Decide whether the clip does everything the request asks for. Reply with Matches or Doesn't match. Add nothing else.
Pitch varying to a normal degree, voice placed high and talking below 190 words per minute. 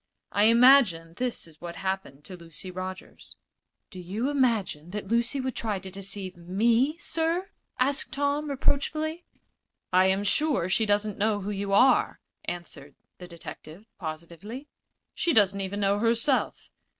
Doesn't match